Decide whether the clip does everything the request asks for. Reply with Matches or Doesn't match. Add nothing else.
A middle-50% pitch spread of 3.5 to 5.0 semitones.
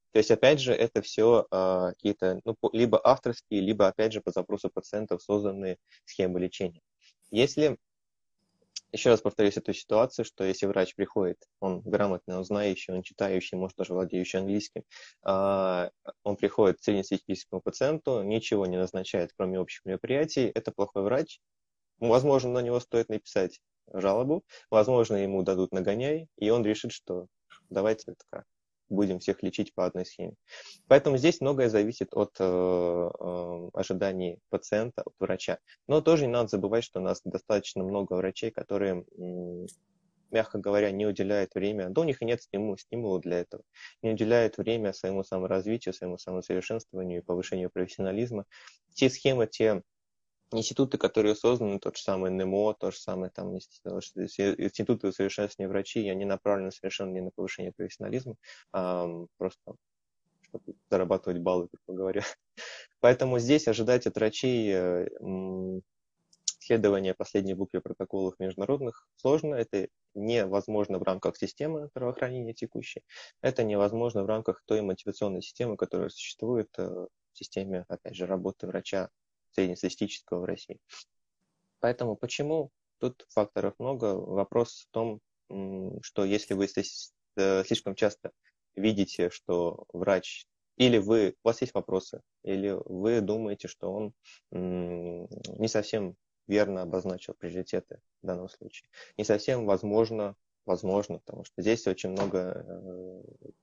Doesn't match